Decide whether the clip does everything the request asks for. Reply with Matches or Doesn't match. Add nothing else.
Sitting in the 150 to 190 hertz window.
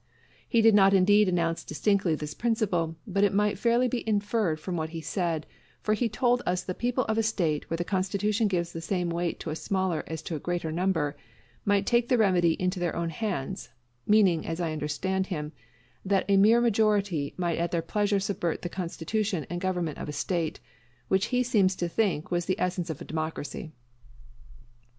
Matches